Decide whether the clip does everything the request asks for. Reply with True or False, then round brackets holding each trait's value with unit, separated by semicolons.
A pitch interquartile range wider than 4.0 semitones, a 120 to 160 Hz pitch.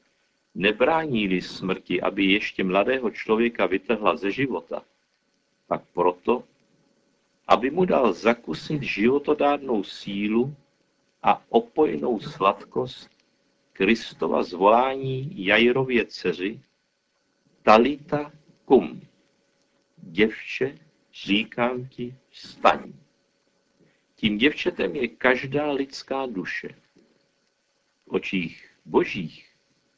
True (5.0 semitones; 125 Hz)